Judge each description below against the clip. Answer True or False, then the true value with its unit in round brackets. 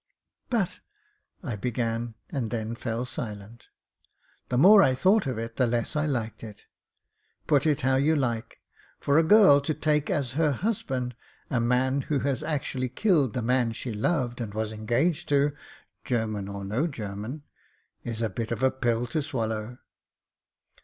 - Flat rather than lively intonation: False (4.3 semitones)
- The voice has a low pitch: True (125 Hz)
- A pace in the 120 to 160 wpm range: False (175 wpm)